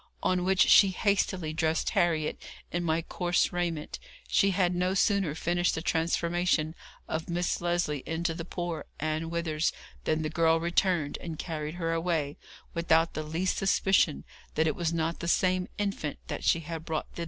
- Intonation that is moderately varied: No, narrow, 1.8 semitones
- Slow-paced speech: No, average, 170 wpm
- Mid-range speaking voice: Yes, medium, 170 Hz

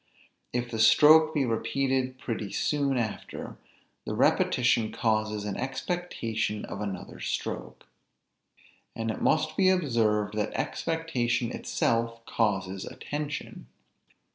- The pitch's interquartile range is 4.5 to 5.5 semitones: Yes, average, 5.0 semitones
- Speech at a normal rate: No, slow, 115 wpm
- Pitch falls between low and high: No, low, 120 Hz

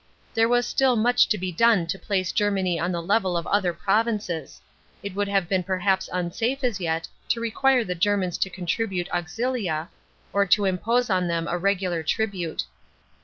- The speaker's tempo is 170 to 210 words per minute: Yes, average, 180 wpm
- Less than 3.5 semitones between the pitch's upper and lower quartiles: No, average, 4.0 semitones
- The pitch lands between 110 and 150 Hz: No, high, 190 Hz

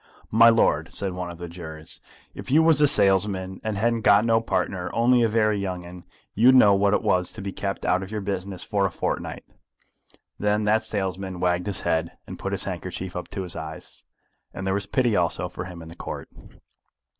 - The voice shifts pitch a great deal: No, average, 3.2 semitones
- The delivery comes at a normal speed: No, fast, 215 wpm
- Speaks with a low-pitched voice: Yes, very low, 95 Hz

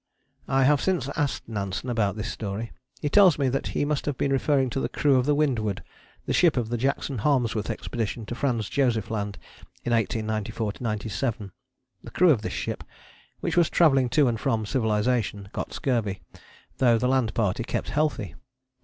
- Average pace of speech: Yes, average, 180 wpm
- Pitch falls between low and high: No, low, 120 Hz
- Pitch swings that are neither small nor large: Yes, average, 4.2 semitones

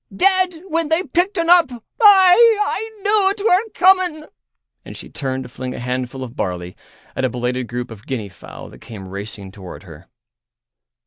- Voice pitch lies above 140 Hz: No, low, 135 Hz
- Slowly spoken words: No, average, 175 wpm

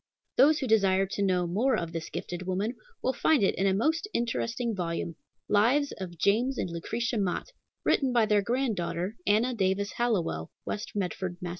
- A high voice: Yes, high, 205 Hz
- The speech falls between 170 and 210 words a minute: Yes, average, 175 wpm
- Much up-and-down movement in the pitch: No, average, 4.6 semitones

